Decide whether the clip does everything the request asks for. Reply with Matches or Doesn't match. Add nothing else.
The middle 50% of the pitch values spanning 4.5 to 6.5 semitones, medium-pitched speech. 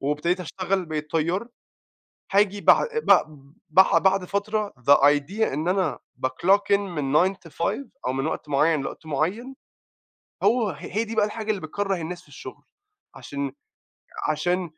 Matches